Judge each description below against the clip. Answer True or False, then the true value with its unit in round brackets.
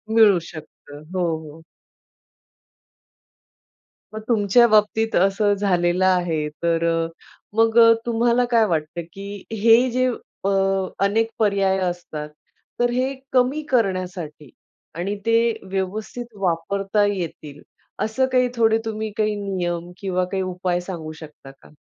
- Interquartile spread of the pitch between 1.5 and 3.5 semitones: False (4.2 semitones)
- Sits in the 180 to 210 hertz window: True (195 Hz)